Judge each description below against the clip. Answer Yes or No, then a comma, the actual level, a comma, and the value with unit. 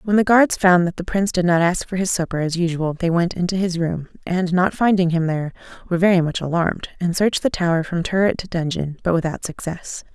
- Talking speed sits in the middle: No, fast, 235 wpm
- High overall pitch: No, medium, 175 Hz